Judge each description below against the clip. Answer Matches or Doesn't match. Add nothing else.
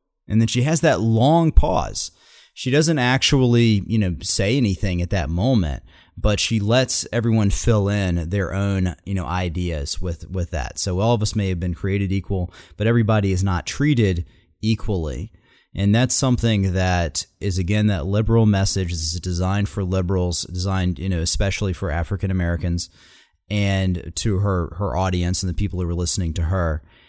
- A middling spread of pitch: Matches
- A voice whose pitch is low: Matches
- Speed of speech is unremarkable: Matches